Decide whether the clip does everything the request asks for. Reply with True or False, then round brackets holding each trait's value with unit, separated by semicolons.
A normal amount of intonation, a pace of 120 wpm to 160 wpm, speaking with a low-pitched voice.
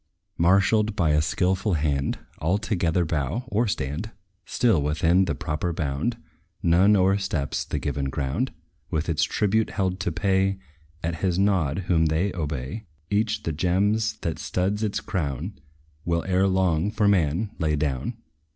True (4.6 semitones; 150 wpm; 90 Hz)